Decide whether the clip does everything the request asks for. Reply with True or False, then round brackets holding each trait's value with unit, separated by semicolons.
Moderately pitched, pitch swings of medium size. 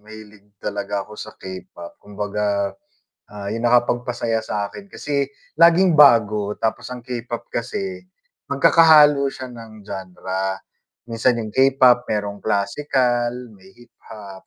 False (110 Hz; 3.7 semitones)